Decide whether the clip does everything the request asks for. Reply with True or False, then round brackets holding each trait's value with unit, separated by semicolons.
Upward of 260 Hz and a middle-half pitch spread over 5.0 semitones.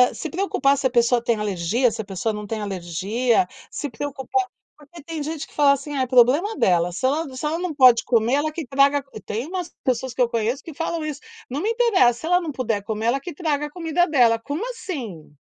True (270 Hz; 5.4 semitones)